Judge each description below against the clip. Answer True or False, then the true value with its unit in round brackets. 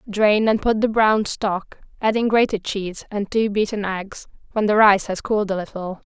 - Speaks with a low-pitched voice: False (205 Hz)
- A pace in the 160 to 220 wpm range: True (195 wpm)